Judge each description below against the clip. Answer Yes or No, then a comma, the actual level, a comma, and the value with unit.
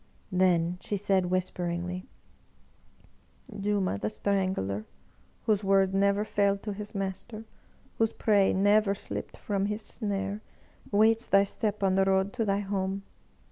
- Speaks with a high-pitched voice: Yes, high, 195 Hz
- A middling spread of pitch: No, narrow, 1.6 semitones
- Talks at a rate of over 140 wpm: No, slow, 135 wpm